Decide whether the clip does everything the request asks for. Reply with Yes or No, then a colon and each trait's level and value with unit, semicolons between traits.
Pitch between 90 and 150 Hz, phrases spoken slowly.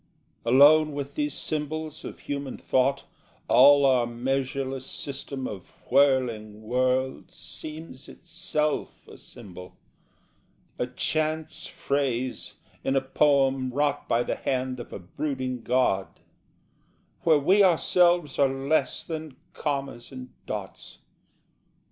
Yes: low, 135 Hz; slow, 110 wpm